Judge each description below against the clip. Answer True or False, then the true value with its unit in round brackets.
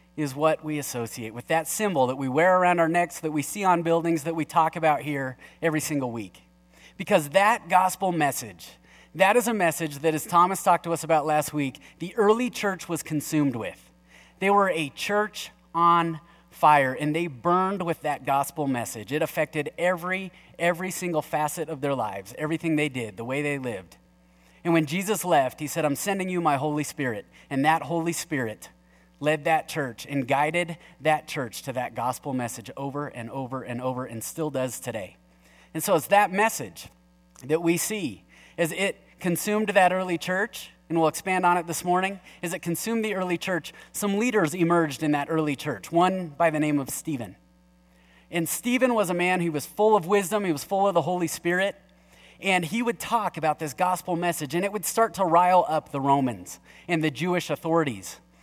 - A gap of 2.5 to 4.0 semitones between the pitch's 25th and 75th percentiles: False (4.6 semitones)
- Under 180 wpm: False (195 wpm)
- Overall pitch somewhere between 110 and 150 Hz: False (160 Hz)